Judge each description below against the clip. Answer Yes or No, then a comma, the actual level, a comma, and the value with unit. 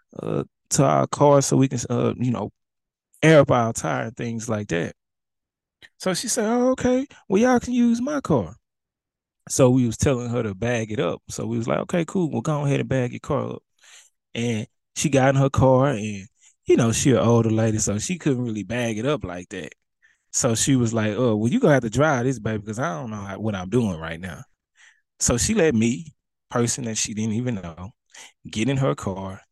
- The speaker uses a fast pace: Yes, fast, 225 wpm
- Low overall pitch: Yes, low, 120 Hz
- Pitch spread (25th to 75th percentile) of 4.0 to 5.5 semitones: Yes, average, 4.3 semitones